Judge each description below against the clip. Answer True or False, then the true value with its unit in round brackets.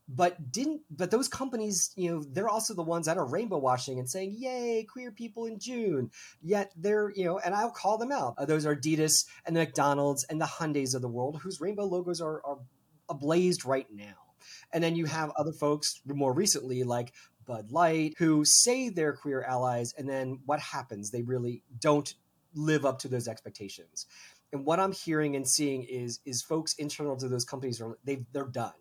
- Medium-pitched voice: True (150 Hz)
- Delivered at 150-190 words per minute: False (200 wpm)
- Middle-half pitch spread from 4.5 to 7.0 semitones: True (5.1 semitones)